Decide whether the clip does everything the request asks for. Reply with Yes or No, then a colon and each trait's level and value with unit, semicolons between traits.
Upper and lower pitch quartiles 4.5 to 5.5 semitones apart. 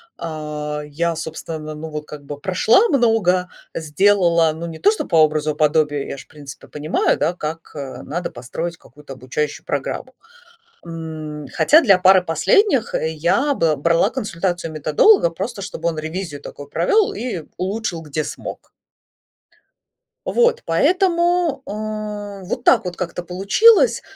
Yes: average, 5.2 semitones